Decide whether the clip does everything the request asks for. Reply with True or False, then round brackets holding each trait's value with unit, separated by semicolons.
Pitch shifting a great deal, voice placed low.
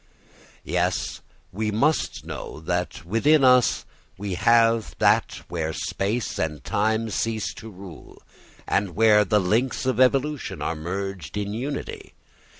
False (4.4 semitones; 105 Hz)